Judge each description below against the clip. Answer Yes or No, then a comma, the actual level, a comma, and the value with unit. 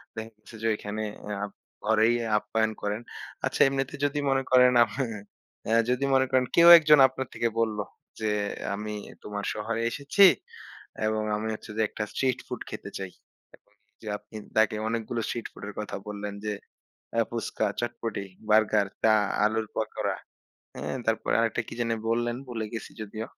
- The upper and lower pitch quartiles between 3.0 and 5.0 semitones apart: No, narrow, 2.4 semitones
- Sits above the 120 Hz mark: No, low, 110 Hz